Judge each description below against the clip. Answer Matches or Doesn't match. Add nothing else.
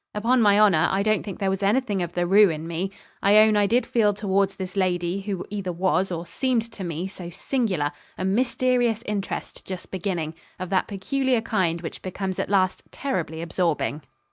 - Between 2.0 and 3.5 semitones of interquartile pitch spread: Matches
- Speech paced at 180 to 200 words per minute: Matches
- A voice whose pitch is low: Doesn't match